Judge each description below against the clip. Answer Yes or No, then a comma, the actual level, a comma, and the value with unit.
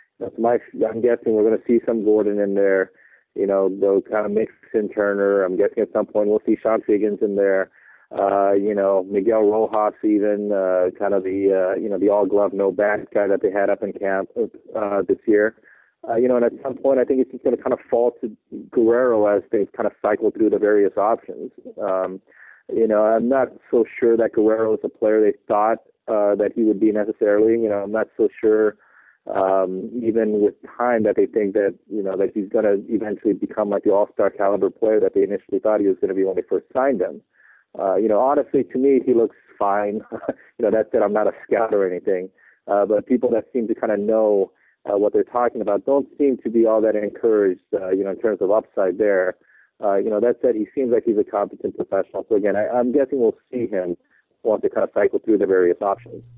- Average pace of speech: No, fast, 235 wpm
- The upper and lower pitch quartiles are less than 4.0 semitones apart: No, average, 5.3 semitones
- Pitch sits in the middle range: No, low, 110 Hz